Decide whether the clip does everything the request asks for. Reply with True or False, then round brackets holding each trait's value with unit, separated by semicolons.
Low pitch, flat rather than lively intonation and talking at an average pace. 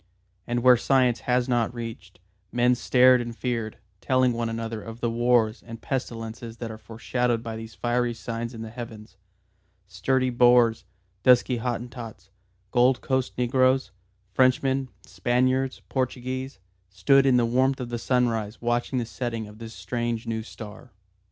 True (120 Hz; 1.8 semitones; 150 wpm)